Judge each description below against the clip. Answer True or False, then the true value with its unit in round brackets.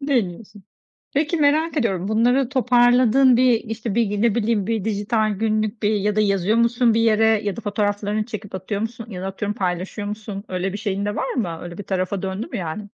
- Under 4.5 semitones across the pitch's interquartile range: True (2.7 semitones)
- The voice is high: True (215 Hz)